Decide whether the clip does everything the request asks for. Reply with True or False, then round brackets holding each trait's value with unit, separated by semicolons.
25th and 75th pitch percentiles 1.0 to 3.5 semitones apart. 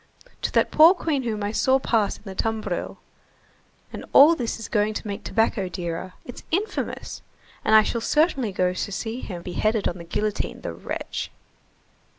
False (4.2 semitones)